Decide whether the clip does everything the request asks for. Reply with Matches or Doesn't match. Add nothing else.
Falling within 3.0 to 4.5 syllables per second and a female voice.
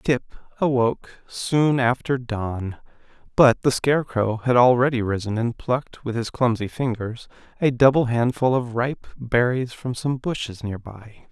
Doesn't match